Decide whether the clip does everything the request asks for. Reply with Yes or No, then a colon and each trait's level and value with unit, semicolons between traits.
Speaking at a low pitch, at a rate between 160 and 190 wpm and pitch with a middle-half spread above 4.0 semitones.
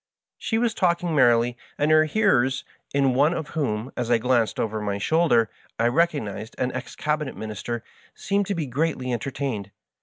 Yes: low, 130 Hz; average, 170 wpm; average, 5.2 semitones